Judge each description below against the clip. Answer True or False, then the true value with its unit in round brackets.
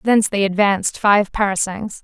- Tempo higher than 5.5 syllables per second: False (5.2 syllables/s)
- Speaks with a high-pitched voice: True (200 Hz)